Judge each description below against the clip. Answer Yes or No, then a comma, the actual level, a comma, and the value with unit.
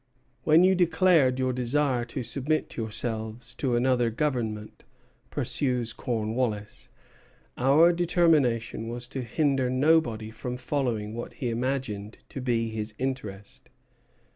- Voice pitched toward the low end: Yes, low, 125 Hz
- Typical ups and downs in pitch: Yes, average, 3.5 semitones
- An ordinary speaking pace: No, slow, 115 wpm